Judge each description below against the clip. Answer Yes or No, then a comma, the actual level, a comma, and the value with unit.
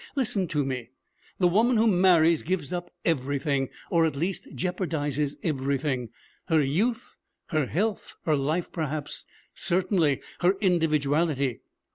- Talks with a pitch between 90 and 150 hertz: No, medium, 160 Hz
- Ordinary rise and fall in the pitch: Yes, average, 4.4 semitones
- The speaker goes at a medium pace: No, slow, 125 wpm